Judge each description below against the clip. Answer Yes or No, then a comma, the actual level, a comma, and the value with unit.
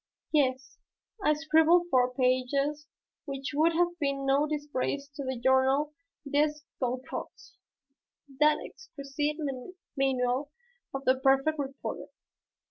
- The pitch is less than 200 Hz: No, very high, 280 Hz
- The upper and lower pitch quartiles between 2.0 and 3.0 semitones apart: Yes, narrow, 2.4 semitones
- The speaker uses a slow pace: Yes, slow, 110 wpm